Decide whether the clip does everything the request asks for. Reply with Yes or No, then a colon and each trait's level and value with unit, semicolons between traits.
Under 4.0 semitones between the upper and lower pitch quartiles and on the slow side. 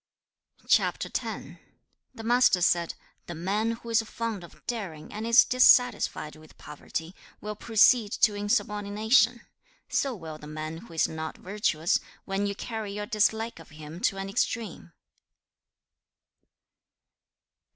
No: average, 5.3 semitones; slow, 130 wpm